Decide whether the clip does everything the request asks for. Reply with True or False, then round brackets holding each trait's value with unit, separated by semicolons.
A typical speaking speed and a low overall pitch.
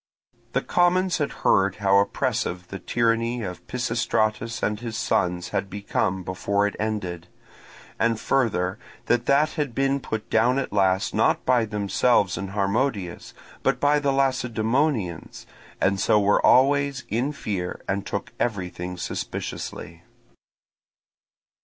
False (130 wpm; 110 Hz)